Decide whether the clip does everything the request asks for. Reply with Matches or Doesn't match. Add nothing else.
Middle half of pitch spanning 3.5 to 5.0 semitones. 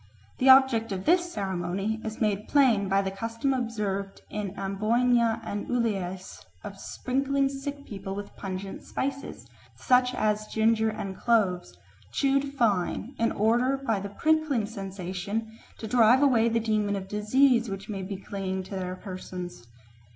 Matches